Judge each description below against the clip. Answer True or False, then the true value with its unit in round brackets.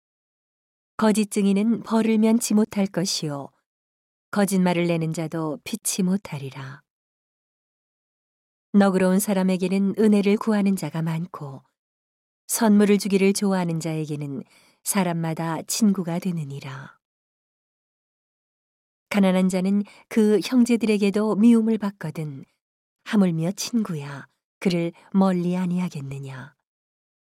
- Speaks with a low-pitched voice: False (190 Hz)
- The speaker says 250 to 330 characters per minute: False (235 characters per minute)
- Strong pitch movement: False (4.2 semitones)